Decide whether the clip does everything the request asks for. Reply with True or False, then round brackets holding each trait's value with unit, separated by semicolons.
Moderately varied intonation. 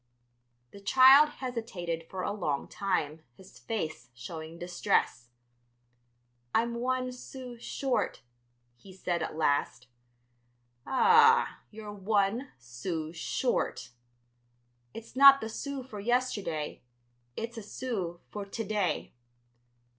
False (6.9 semitones)